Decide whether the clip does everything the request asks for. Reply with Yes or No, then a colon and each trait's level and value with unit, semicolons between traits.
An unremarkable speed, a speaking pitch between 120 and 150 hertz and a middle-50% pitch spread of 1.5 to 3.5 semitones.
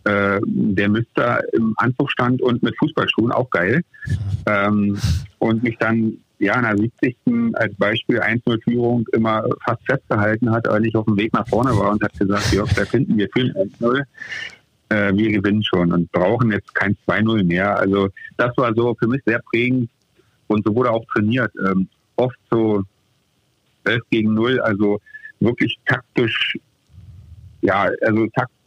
No: average, 165 wpm; low, 110 Hz; narrow, 2.6 semitones